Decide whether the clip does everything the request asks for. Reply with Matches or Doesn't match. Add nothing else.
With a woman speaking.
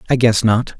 Doesn't match